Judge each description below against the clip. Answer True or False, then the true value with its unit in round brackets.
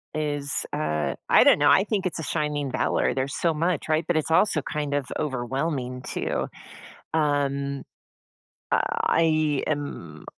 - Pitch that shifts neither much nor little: False (2.2 semitones)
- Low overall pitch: False (145 Hz)